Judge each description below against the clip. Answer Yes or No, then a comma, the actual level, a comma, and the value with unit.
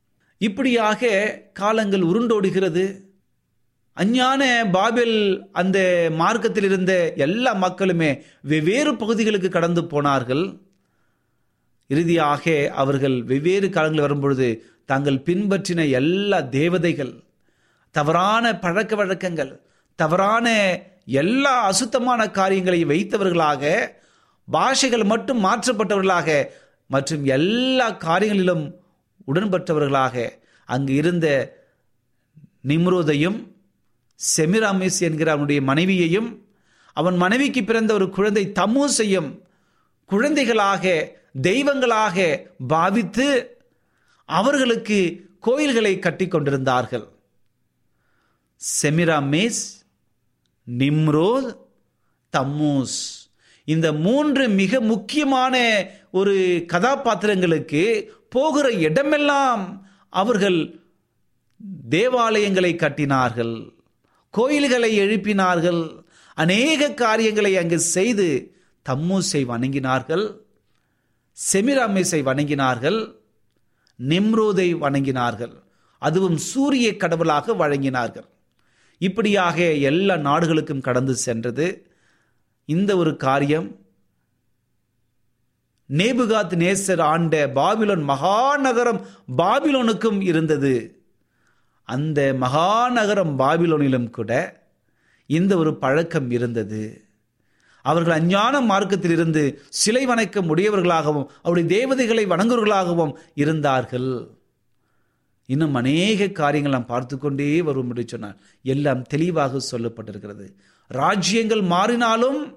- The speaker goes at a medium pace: No, slow, 70 wpm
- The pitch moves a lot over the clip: Yes, wide, 7.1 semitones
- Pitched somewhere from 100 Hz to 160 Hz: No, medium, 175 Hz